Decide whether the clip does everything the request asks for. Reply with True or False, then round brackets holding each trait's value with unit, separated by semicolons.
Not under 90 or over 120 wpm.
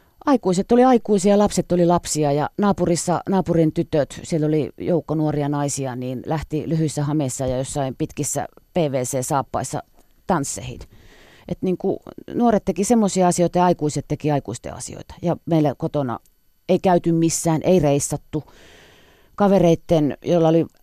False (135 wpm)